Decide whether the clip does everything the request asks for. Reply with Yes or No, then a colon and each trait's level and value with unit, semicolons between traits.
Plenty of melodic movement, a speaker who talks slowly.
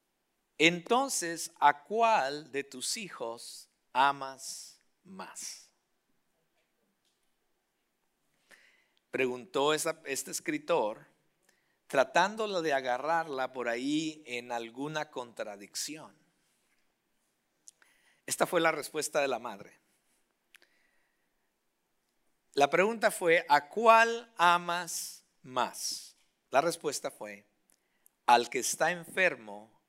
Yes: wide, 5.7 semitones; slow, 80 wpm